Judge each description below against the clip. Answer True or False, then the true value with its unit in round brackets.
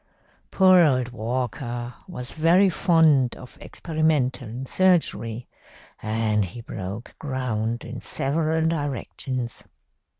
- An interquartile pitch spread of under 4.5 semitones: False (5.2 semitones)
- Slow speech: True (95 wpm)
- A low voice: True (130 Hz)